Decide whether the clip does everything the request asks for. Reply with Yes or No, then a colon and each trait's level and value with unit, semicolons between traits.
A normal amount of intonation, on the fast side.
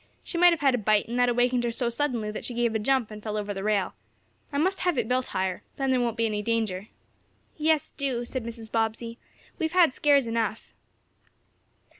Yes: average, 3.7 semitones; fast, 215 wpm